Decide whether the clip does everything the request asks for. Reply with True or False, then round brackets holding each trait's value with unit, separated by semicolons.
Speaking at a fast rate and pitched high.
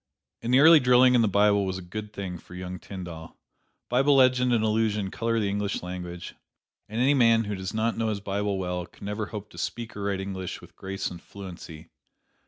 False (210 wpm; 105 Hz)